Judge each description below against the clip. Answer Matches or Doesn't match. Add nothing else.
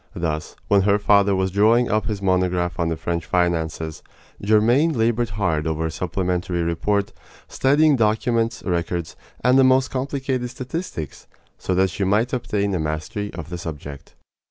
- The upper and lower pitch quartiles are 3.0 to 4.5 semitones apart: Doesn't match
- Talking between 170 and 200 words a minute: Doesn't match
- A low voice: Matches